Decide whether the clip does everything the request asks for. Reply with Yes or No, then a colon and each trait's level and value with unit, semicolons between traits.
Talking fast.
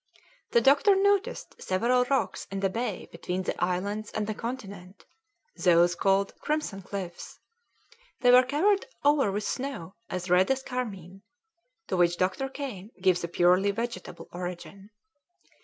No: average, 140 wpm